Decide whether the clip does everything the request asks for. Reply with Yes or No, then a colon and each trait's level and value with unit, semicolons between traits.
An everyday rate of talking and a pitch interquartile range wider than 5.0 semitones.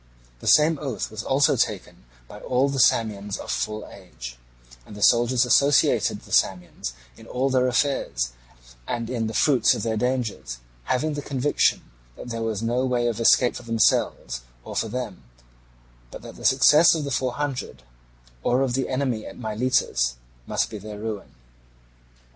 No: average, 170 wpm; average, 3.6 semitones